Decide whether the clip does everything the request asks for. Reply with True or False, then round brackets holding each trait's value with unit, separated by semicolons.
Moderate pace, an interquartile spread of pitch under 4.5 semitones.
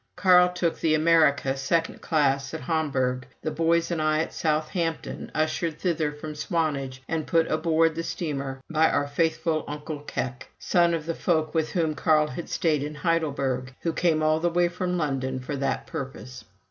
True (175 wpm; 2.7 semitones)